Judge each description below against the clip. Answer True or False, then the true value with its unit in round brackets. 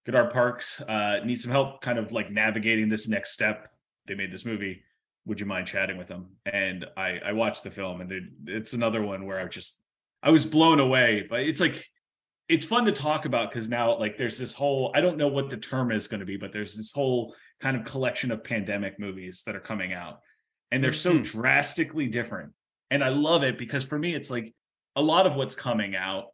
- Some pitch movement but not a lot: True (4.9 semitones)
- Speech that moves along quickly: True (225 wpm)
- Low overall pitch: True (115 Hz)